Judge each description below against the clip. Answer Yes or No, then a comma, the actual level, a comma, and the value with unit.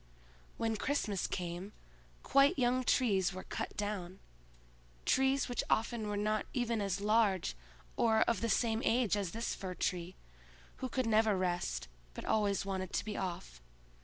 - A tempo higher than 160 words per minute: No, average, 155 wpm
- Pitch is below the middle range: No, high, 210 Hz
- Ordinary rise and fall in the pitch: Yes, average, 3.7 semitones